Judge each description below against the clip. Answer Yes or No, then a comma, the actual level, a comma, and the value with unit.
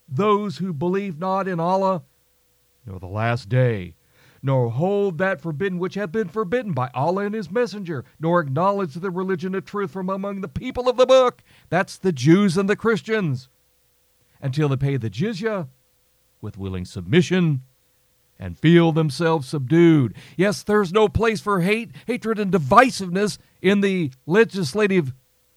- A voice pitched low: No, medium, 180 Hz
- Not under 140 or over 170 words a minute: Yes, average, 155 wpm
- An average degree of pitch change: No, wide, 7.0 semitones